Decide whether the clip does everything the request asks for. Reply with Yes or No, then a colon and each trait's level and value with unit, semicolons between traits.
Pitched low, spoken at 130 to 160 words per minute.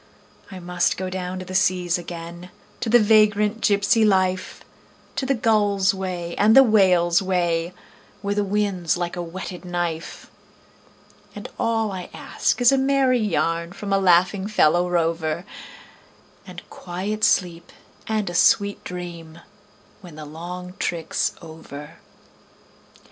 No: medium, 185 Hz; average, 140 wpm